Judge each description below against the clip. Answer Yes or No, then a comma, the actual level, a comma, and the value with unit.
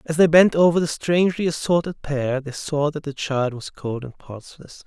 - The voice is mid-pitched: Yes, medium, 150 Hz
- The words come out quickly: Yes, fast, 210 wpm